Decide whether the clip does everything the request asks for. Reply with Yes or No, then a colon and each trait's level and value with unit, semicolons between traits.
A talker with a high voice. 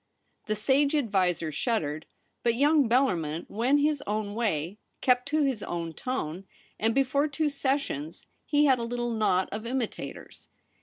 Yes: high, 235 Hz